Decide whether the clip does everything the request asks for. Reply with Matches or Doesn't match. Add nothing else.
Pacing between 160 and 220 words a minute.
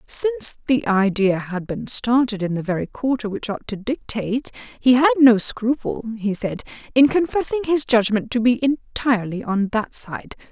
Matches